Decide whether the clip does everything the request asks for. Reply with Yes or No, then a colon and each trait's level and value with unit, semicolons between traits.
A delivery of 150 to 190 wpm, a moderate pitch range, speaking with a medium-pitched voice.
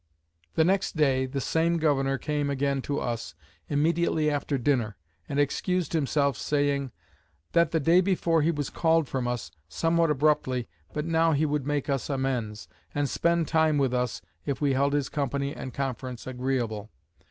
Yes: average, 165 wpm; average, 3.2 semitones; medium, 145 Hz